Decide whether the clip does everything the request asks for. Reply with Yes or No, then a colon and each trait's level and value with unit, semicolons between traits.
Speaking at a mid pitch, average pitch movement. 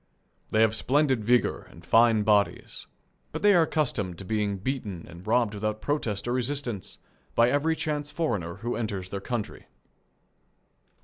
No: low, 110 Hz; average, 5.0 semitones